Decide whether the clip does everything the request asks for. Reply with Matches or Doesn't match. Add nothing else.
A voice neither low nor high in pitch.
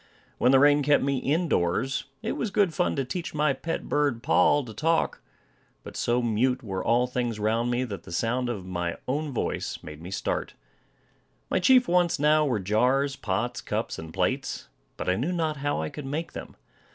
Doesn't match